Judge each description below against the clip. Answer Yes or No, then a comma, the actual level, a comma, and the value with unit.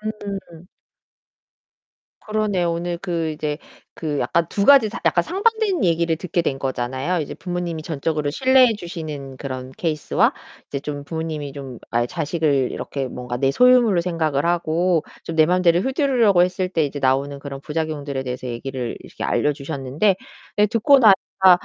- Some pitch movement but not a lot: Yes, average, 4.9 semitones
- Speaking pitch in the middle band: Yes, medium, 165 Hz